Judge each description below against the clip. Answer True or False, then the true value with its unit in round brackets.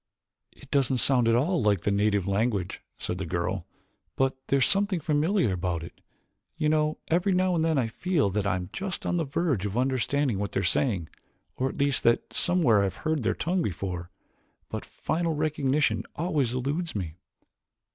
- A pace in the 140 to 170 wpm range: False (190 wpm)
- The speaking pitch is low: True (130 Hz)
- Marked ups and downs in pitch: True (7.7 semitones)